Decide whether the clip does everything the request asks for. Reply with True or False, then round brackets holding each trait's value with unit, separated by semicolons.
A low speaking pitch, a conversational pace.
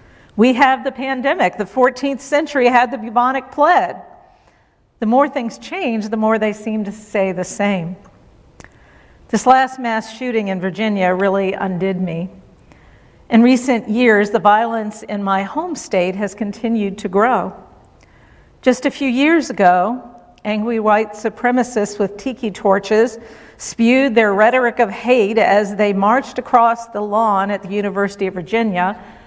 False (225 Hz; 150 wpm)